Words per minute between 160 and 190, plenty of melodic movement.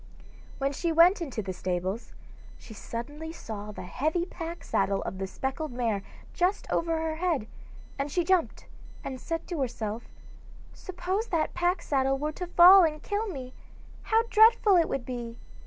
Yes: average, 165 wpm; wide, 6.7 semitones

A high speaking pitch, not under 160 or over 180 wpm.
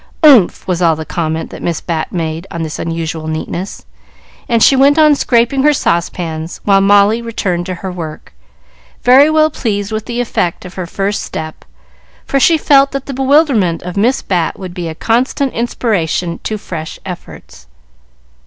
Yes: high, 195 Hz; average, 170 wpm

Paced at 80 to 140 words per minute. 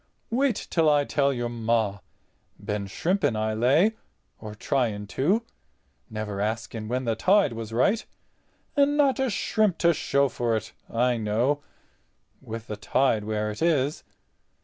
Yes: slow, 135 wpm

